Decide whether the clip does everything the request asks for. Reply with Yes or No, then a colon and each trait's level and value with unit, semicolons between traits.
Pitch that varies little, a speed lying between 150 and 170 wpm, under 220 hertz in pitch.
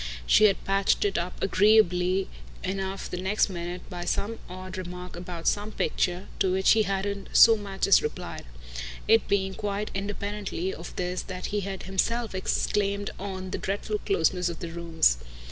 Yes: narrow, 2.0 semitones; average, 165 wpm; high, 190 Hz